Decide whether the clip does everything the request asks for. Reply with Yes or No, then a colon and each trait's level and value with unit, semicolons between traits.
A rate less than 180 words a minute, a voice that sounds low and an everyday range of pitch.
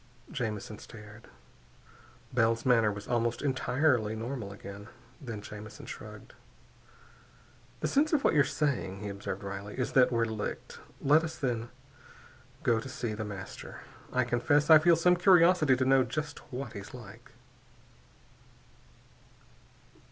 Yes: slow, 135 wpm; low, 120 Hz; average, 4.8 semitones